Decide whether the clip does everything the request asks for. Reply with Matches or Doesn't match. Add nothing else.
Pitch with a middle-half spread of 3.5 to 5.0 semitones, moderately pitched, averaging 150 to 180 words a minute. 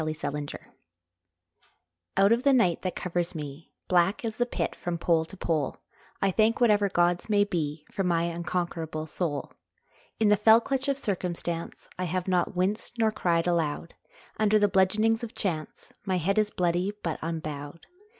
Matches